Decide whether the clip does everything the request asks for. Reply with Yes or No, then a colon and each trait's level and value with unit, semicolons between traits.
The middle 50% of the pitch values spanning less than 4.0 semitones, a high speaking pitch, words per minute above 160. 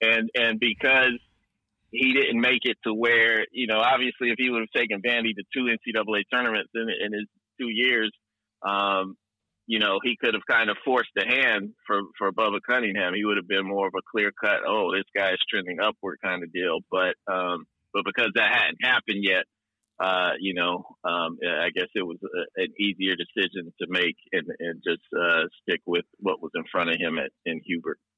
No: average, 3.3 semitones; low, 110 Hz; fast, 205 wpm